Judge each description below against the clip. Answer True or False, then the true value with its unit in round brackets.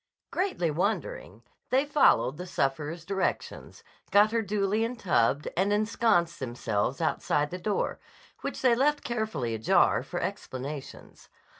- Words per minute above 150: False (135 wpm)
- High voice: False (180 Hz)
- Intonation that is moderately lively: False (7.5 semitones)